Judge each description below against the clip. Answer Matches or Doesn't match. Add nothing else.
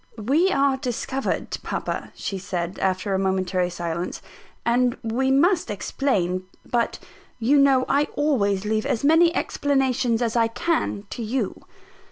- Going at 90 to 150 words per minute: Matches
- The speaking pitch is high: Matches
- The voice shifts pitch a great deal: Matches